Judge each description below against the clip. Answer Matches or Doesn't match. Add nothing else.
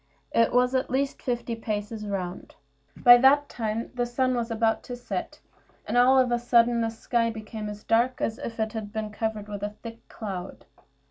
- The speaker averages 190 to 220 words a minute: Matches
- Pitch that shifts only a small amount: Matches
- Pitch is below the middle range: Doesn't match